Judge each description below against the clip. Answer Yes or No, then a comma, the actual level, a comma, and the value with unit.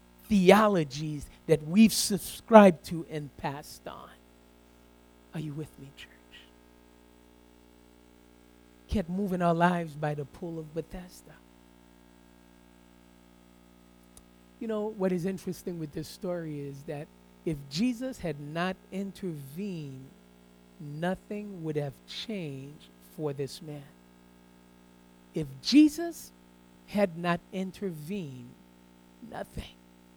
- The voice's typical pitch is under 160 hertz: Yes, medium, 140 Hz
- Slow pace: Yes, slow, 100 wpm